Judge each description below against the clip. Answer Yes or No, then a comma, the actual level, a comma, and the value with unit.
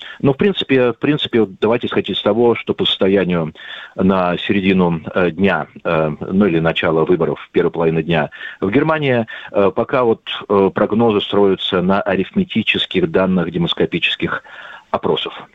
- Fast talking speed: No, average, 130 wpm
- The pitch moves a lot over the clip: Yes, wide, 6.8 semitones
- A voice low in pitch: Yes, low, 100 Hz